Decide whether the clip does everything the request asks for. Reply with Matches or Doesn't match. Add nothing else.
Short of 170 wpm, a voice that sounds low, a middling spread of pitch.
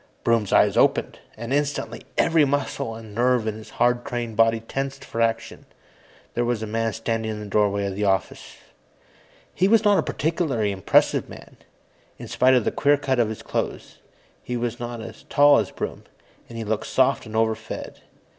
Doesn't match